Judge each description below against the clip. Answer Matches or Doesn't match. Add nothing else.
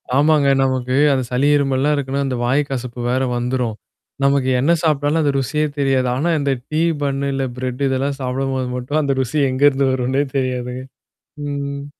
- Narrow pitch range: Matches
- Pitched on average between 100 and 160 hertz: Matches